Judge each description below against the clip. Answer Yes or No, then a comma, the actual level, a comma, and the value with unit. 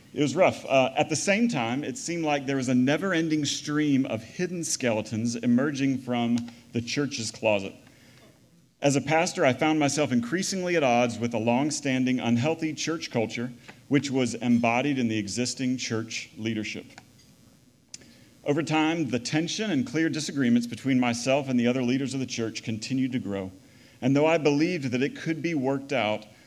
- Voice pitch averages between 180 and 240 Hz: No, low, 130 Hz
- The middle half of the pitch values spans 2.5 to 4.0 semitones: No, average, 4.4 semitones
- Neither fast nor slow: Yes, average, 175 wpm